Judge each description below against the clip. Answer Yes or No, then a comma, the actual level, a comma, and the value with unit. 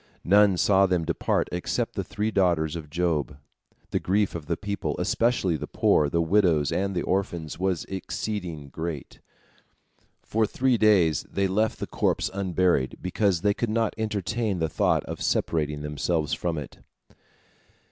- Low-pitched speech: Yes, very low, 90 Hz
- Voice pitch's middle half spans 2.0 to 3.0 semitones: No, average, 4.1 semitones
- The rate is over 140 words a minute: Yes, average, 155 wpm